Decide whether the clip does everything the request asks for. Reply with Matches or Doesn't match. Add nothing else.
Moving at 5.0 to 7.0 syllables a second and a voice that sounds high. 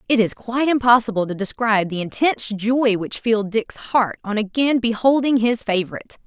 Matches